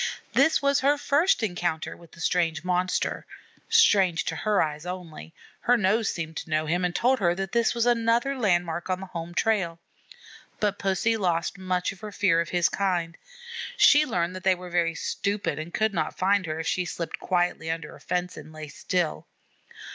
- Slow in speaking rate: No, average, 190 wpm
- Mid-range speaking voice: Yes, medium, 180 Hz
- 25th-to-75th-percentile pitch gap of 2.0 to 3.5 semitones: No, average, 3.9 semitones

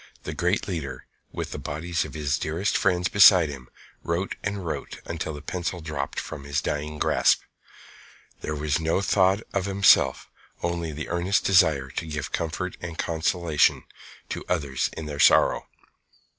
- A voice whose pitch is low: Yes, very low, 80 Hz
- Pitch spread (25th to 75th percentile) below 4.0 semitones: Yes, average, 3.2 semitones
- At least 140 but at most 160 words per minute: Yes, average, 155 wpm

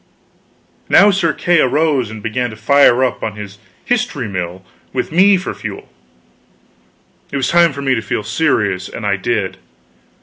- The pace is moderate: Yes, average, 165 wpm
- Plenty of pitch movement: Yes, wide, 7.3 semitones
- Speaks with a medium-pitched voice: No, low, 125 Hz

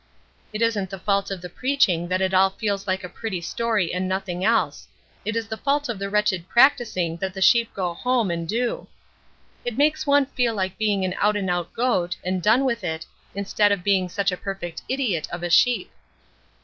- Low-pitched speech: No, high, 200 Hz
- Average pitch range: Yes, average, 4.0 semitones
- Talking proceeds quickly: Yes, fast, 210 wpm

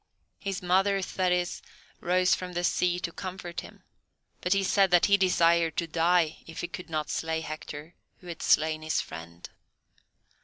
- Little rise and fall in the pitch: Yes, narrow, 2.2 semitones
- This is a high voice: No, medium, 175 Hz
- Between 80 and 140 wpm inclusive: No, average, 165 wpm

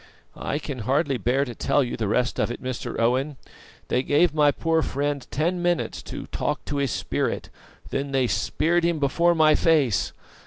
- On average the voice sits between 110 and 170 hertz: Yes, medium, 140 Hz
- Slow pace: No, average, 180 wpm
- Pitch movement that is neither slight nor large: Yes, average, 3.6 semitones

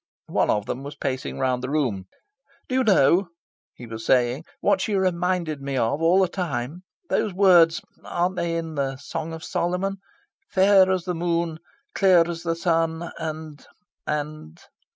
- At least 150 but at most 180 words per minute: Yes, average, 165 wpm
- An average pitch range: Yes, average, 4.5 semitones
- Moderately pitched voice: Yes, medium, 165 Hz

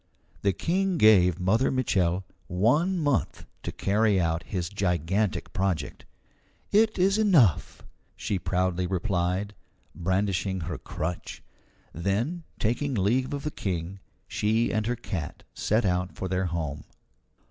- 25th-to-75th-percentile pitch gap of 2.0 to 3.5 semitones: No, average, 4.9 semitones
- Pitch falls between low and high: No, very low, 95 Hz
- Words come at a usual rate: No, slow, 125 wpm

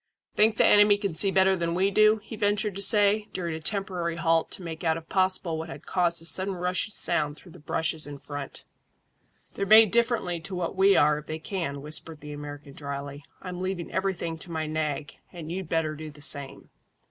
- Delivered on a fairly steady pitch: No, average, 3.9 semitones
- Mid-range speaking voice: Yes, medium, 170 Hz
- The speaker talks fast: Yes, fast, 210 wpm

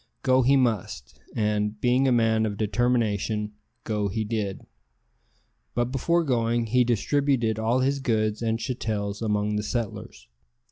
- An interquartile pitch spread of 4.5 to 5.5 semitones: No, average, 2.8 semitones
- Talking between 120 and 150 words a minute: Yes, average, 140 wpm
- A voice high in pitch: No, low, 115 Hz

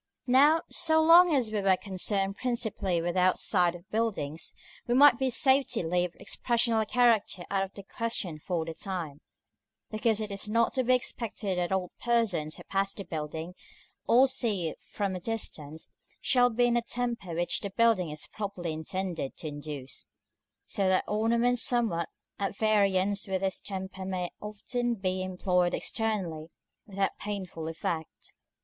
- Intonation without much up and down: No, average, 4.6 semitones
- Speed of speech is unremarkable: Yes, average, 165 wpm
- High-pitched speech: Yes, high, 195 Hz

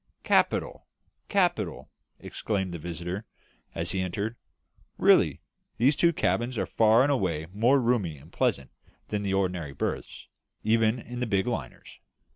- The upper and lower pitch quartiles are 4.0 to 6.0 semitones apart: Yes, average, 5.3 semitones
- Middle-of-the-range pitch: No, low, 105 Hz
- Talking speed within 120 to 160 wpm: Yes, average, 140 wpm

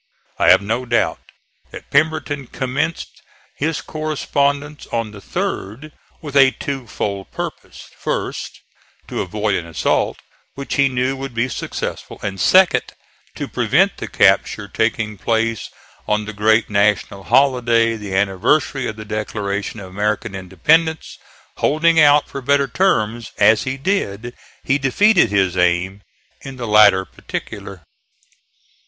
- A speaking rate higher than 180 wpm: No, slow, 135 wpm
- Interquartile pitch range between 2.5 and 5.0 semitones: No, wide, 5.5 semitones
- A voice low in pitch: Yes, low, 115 Hz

